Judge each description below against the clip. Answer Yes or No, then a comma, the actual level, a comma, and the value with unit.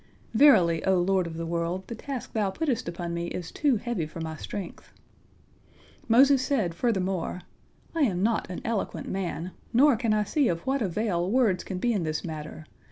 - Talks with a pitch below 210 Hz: Yes, high, 190 Hz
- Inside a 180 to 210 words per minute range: Yes, average, 185 wpm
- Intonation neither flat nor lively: No, wide, 5.7 semitones